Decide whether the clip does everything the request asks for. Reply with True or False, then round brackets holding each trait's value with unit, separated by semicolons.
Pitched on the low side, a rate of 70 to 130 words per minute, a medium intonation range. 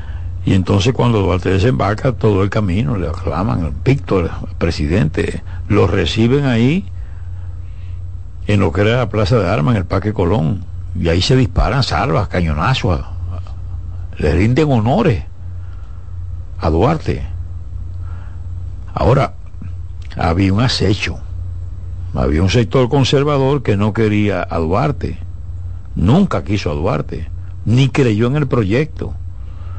True (90 Hz; 125 wpm; 4.0 semitones)